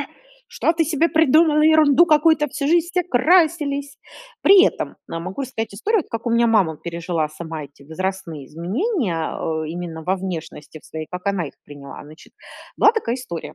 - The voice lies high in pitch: Yes, high, 225 Hz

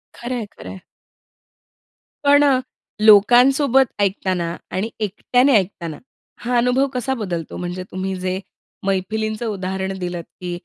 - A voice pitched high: Yes, high, 205 Hz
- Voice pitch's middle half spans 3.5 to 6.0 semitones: Yes, average, 4.8 semitones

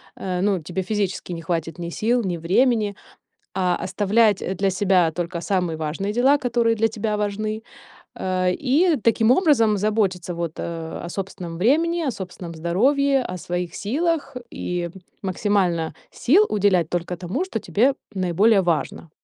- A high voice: Yes, high, 195 Hz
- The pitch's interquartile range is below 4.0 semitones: No, average, 4.5 semitones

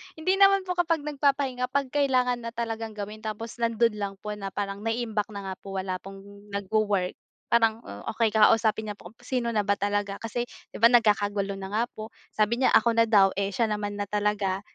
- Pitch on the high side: Yes, high, 215 Hz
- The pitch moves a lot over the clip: No, average, 2.7 semitones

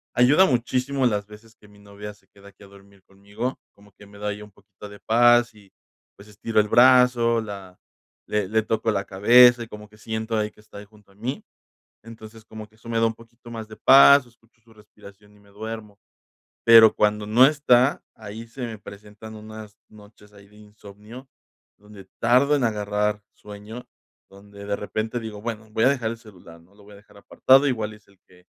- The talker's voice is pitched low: Yes, low, 105 Hz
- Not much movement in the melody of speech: Yes, narrow, 2.1 semitones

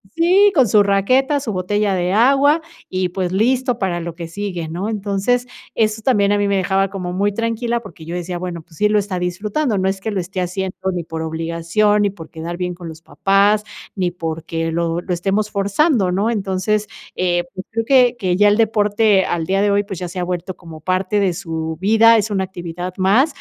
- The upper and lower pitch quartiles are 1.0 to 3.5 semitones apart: Yes, average, 3.2 semitones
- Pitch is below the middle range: No, high, 195 Hz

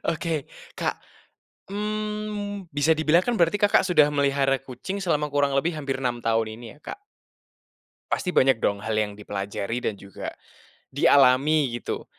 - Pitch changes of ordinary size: No, wide, 6.4 semitones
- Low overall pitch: No, medium, 145 Hz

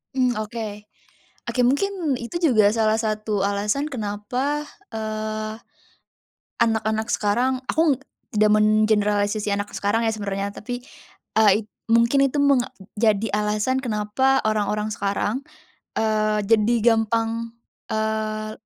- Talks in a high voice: Yes, high, 220 Hz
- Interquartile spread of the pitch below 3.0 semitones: Yes, narrow, 2.5 semitones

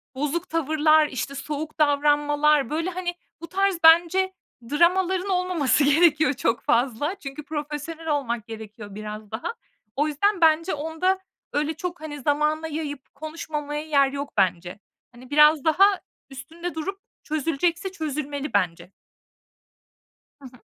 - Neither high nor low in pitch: No, very high, 300 Hz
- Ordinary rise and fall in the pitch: Yes, average, 3.0 semitones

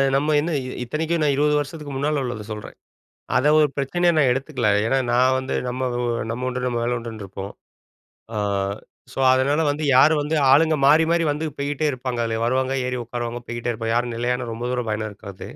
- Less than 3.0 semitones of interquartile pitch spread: No, average, 3.8 semitones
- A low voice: Yes, low, 130 Hz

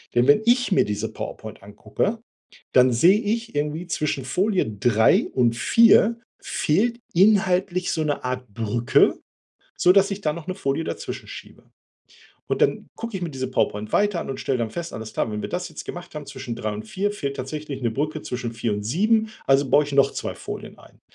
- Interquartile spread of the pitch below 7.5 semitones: No, wide, 7.8 semitones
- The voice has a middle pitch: Yes, medium, 150 Hz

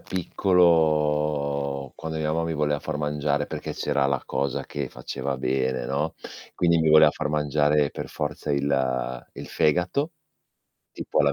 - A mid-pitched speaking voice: No, very low, 75 Hz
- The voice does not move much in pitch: Yes, narrow, 2.0 semitones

